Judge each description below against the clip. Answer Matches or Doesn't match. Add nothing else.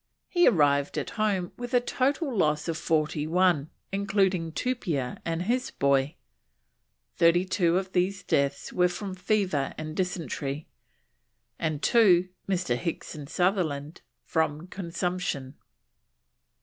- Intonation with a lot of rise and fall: Doesn't match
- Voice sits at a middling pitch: Matches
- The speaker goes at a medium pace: Doesn't match